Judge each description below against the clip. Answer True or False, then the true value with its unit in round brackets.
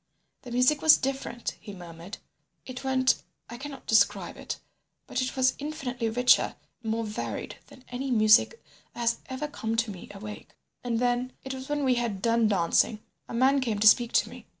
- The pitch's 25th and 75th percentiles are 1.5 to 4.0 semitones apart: True (3.0 semitones)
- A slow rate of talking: False (175 wpm)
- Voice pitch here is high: True (245 Hz)